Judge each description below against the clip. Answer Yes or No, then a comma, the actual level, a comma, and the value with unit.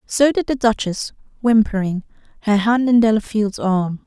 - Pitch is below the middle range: No, high, 220 Hz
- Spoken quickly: No, average, 150 wpm